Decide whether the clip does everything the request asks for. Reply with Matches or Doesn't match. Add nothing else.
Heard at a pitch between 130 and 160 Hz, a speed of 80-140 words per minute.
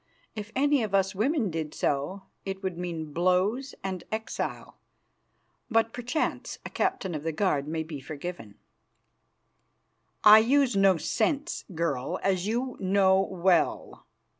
Doesn't match